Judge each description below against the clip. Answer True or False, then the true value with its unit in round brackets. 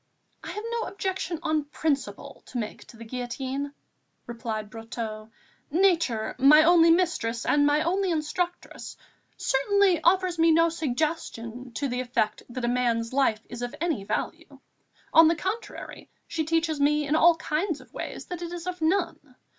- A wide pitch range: True (5.7 semitones)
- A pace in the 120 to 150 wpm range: False (160 wpm)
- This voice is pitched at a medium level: False (300 Hz)